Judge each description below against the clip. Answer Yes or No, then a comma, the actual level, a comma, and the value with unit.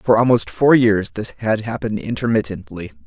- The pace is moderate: Yes, average, 155 wpm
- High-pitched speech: No, low, 110 Hz